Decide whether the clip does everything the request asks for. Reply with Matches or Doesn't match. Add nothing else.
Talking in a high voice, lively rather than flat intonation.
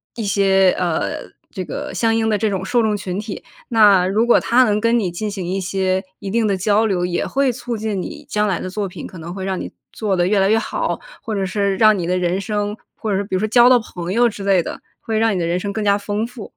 Doesn't match